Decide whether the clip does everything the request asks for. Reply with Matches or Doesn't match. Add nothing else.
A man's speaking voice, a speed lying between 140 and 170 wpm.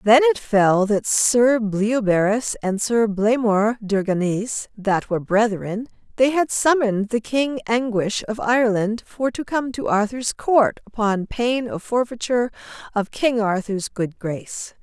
Doesn't match